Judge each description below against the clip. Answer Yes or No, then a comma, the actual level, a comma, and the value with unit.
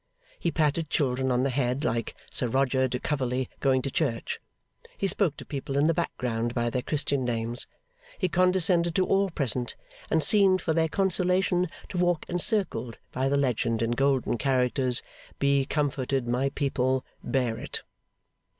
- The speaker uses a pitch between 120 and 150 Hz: Yes, low, 135 Hz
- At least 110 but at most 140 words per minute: No, average, 160 wpm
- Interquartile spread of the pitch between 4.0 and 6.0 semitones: Yes, average, 4.9 semitones